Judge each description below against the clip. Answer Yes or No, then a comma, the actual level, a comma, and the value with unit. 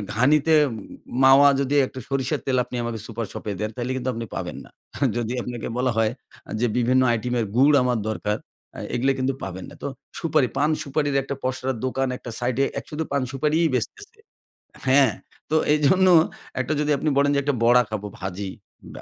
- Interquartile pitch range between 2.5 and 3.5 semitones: Yes, average, 3.2 semitones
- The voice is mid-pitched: No, low, 130 Hz